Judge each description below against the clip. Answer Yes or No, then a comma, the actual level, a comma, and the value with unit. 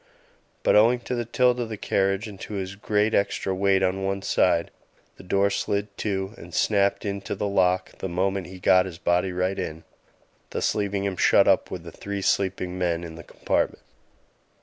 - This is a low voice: Yes, very low, 95 Hz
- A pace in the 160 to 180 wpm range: No, average, 195 wpm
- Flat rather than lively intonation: Yes, narrow, 1.7 semitones